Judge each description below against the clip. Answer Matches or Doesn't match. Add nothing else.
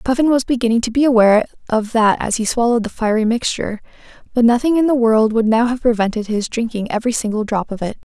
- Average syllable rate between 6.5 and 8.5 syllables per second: Matches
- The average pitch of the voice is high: Matches